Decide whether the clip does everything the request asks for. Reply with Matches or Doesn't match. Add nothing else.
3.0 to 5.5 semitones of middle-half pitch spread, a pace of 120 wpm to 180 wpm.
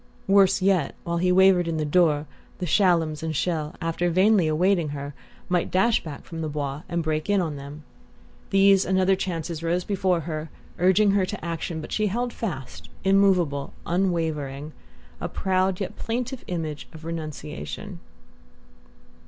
Matches